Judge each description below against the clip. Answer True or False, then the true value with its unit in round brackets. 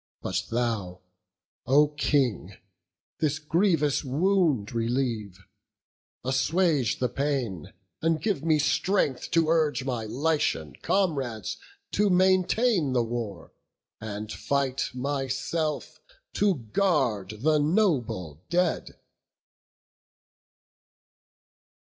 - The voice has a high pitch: False (140 Hz)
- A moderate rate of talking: False (90 wpm)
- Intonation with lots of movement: True (6.1 semitones)